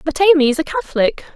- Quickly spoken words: Yes, fast, 220 wpm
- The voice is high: Yes, very high, 310 Hz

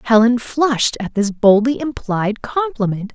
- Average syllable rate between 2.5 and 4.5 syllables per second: Yes, 4.3 syllables/s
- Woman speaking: Yes, female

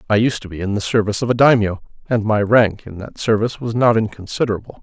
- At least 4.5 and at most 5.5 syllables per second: No, 6.6 syllables/s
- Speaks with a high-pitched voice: No, low, 110 Hz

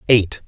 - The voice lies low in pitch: Yes, low, 105 Hz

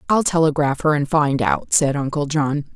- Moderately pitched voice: Yes, medium, 150 Hz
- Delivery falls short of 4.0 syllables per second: No, 4.7 syllables/s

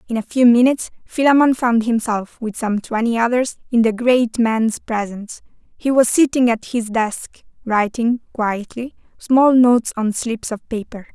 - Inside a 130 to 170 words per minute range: Yes, average, 160 wpm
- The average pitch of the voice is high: Yes, high, 235 Hz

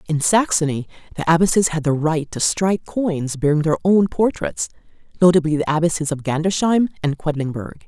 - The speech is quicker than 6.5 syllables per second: No, 5.5 syllables/s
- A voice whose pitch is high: No, medium, 165 Hz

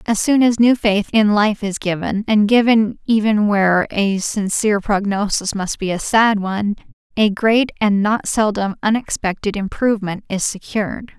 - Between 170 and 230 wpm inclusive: No, average, 160 wpm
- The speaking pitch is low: No, high, 210 Hz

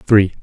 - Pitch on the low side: Yes, low, 100 Hz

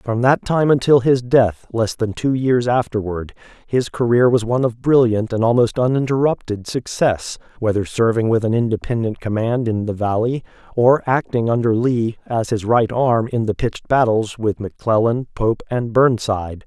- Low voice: Yes, low, 115 Hz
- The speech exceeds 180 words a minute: No, average, 170 wpm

